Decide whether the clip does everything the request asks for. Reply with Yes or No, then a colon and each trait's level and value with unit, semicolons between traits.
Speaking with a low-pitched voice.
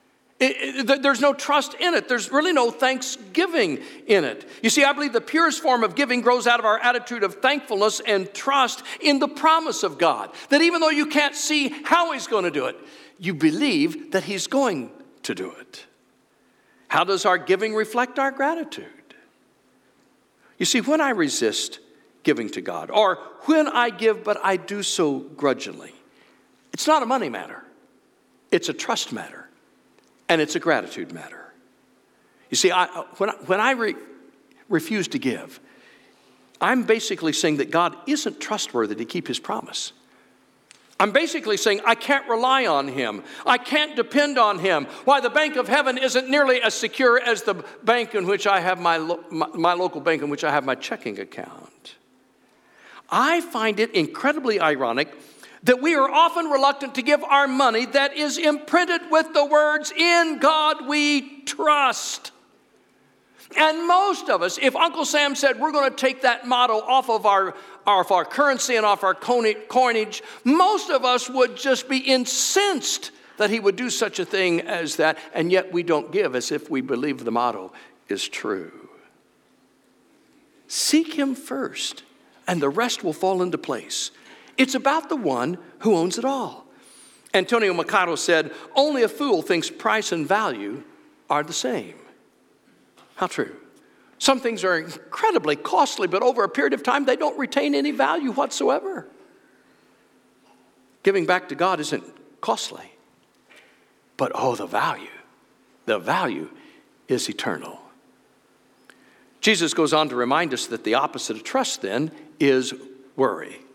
No: very high, 260 Hz